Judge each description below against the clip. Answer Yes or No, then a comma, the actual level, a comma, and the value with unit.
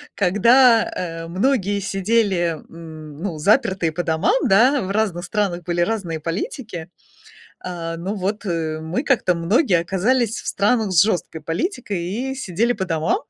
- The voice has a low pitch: No, medium, 185 Hz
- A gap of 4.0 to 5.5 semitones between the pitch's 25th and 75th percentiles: Yes, average, 4.7 semitones